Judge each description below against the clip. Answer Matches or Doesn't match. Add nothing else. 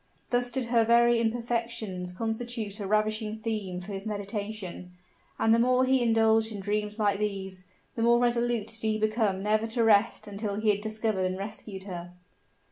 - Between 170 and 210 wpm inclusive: Matches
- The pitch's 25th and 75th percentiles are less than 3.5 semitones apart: Matches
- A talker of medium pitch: Doesn't match